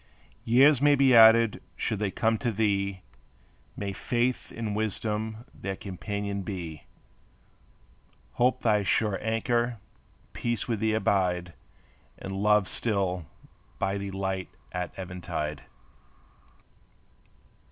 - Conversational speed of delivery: No, slow, 110 wpm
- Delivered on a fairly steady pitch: No, average, 3.0 semitones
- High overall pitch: No, low, 105 Hz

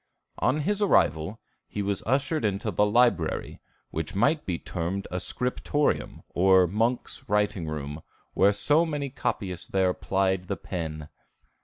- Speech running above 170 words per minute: No, slow, 135 wpm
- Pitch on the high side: No, low, 100 Hz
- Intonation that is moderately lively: No, wide, 5.9 semitones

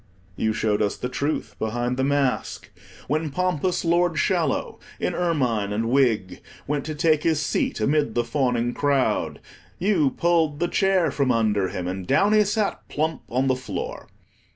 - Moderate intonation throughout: No, wide, 5.7 semitones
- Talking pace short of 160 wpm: No, average, 165 wpm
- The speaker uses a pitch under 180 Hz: Yes, medium, 140 Hz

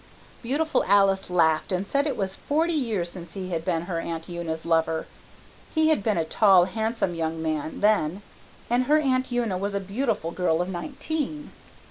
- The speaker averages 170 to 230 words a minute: Yes, average, 180 wpm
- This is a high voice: Yes, high, 195 Hz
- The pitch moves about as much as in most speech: No, wide, 6.6 semitones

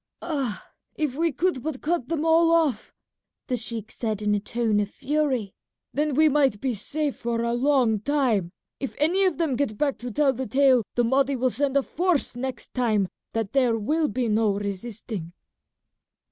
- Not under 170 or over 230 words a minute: Yes, average, 185 wpm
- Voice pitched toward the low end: No, very high, 260 Hz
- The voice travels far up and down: No, average, 4.8 semitones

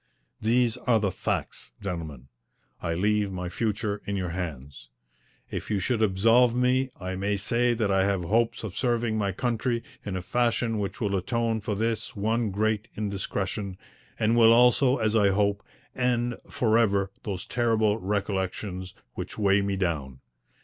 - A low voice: Yes, low, 105 Hz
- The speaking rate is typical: Yes, average, 160 wpm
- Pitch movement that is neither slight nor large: Yes, average, 3.3 semitones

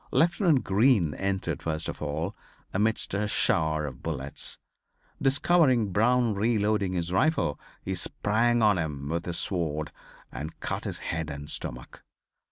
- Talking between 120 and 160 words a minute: Yes, average, 140 wpm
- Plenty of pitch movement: Yes, wide, 6.3 semitones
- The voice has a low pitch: Yes, very low, 95 Hz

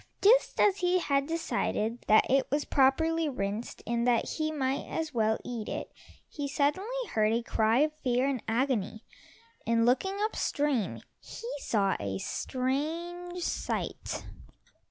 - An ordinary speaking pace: Yes, average, 145 wpm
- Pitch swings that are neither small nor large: No, wide, 5.8 semitones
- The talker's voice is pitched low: No, very high, 270 Hz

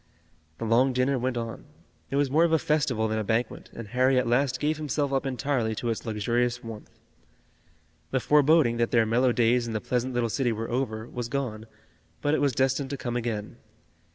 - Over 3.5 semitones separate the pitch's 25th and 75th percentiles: No, average, 2.9 semitones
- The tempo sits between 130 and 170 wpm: No, fast, 205 wpm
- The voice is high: No, low, 125 Hz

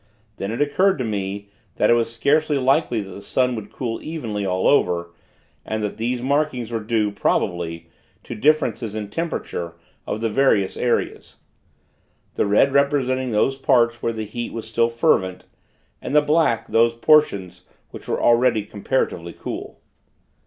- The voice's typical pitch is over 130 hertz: No, low, 115 Hz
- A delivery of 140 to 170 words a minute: Yes, average, 160 wpm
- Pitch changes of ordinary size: Yes, average, 4.4 semitones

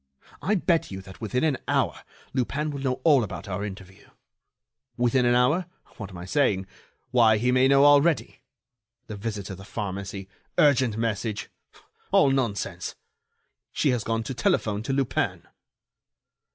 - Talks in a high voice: No, low, 120 Hz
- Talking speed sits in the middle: Yes, average, 150 wpm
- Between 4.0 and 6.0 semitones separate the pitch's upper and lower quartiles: Yes, average, 5.1 semitones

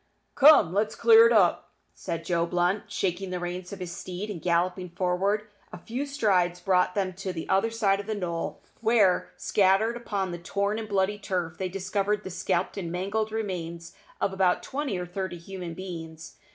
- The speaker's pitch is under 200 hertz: Yes, high, 190 Hz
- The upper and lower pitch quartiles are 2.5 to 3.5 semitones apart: Yes, average, 2.8 semitones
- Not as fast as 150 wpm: No, average, 185 wpm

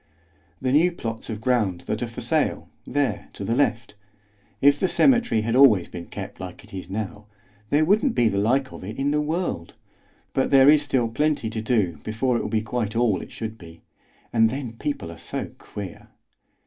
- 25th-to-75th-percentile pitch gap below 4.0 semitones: No, average, 4.8 semitones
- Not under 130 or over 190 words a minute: No, average, 200 wpm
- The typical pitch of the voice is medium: No, low, 115 Hz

